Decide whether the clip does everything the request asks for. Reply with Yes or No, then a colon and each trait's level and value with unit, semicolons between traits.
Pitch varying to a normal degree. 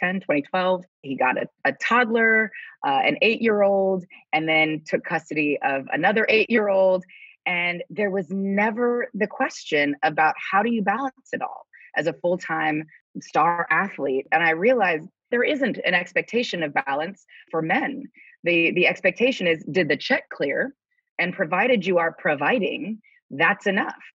No: wide, 6.4 semitones